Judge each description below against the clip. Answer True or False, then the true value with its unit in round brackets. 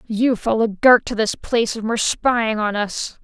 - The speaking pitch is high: True (225 Hz)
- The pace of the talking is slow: False (205 wpm)